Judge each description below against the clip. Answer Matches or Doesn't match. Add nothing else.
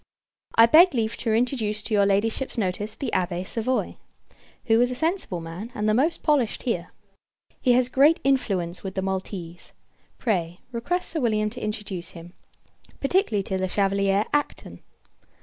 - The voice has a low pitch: Doesn't match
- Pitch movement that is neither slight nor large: Matches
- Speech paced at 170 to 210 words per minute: Doesn't match